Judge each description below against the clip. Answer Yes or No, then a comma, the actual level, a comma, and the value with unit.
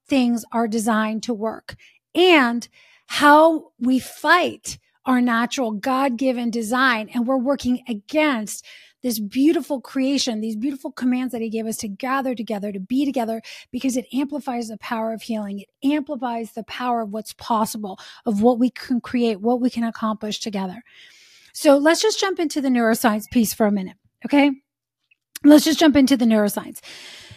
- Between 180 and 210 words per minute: No, average, 165 wpm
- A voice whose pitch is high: Yes, high, 245 Hz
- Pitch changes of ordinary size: Yes, average, 3.8 semitones